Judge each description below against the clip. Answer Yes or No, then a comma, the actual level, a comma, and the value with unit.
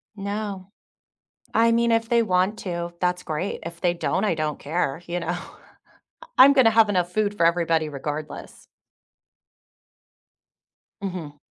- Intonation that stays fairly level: No, average, 4.0 semitones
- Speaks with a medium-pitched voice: Yes, medium, 180 Hz